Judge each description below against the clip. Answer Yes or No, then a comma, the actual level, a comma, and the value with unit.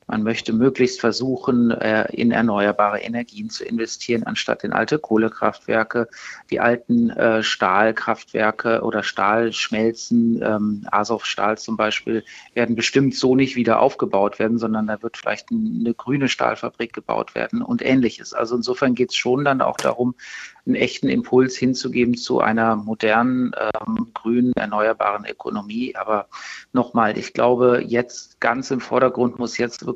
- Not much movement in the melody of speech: Yes, narrow, 2.3 semitones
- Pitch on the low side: Yes, low, 120 Hz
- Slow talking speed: No, average, 135 wpm